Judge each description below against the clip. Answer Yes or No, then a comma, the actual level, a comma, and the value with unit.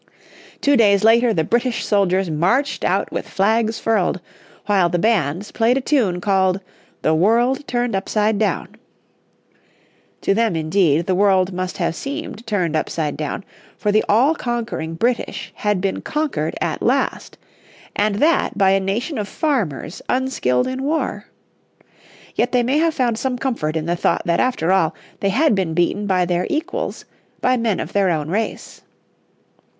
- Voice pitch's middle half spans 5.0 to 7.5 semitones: Yes, wide, 5.4 semitones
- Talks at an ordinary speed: Yes, average, 160 wpm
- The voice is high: Yes, high, 205 Hz